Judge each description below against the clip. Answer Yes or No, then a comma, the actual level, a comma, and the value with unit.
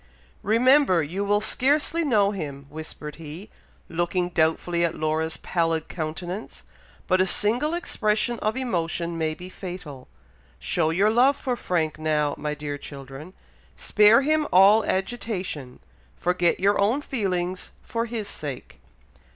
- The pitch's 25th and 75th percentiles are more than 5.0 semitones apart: Yes, wide, 5.4 semitones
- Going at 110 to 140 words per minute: Yes, slow, 135 wpm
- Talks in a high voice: No, medium, 180 Hz